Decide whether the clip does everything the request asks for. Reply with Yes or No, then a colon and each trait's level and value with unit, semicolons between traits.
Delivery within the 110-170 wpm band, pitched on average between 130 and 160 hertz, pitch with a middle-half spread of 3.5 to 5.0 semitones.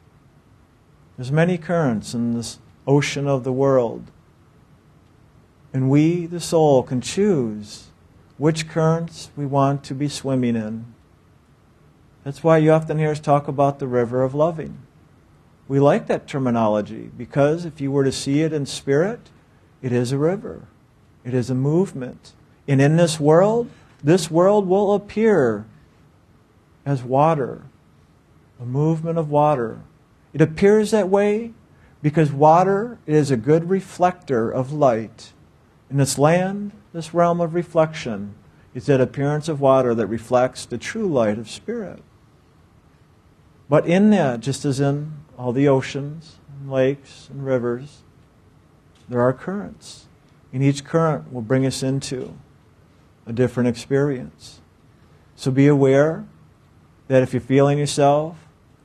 Yes: average, 140 wpm; medium, 140 Hz; average, 4.0 semitones